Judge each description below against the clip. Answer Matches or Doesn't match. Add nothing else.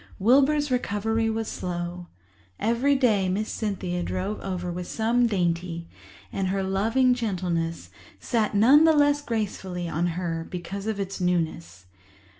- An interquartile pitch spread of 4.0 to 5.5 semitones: Matches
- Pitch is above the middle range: Matches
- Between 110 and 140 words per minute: Matches